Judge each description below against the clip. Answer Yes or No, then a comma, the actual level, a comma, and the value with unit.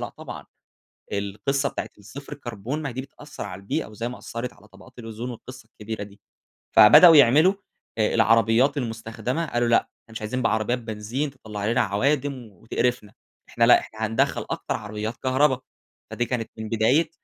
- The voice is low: Yes, low, 115 Hz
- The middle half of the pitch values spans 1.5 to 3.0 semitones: No, average, 3.4 semitones